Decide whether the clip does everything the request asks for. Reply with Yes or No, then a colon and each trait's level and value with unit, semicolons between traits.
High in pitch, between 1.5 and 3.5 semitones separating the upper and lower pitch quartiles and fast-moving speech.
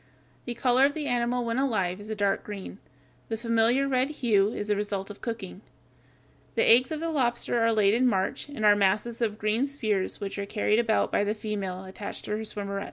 Yes: high, 220 Hz; average, 3.1 semitones; fast, 215 wpm